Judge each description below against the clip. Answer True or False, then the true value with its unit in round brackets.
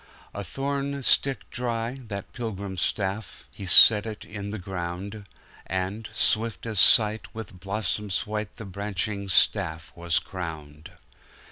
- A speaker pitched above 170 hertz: False (100 Hz)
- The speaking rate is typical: False (125 wpm)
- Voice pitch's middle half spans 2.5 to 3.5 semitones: True (2.9 semitones)